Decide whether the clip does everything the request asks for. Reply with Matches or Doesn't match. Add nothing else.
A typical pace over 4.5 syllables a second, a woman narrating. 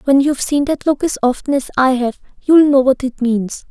Matches